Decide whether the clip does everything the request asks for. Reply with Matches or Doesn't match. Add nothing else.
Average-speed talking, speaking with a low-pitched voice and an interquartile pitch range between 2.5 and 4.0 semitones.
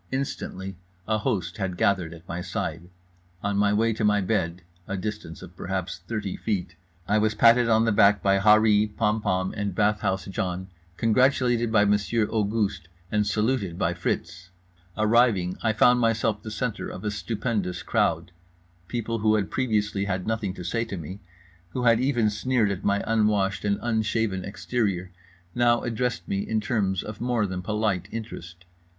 Matches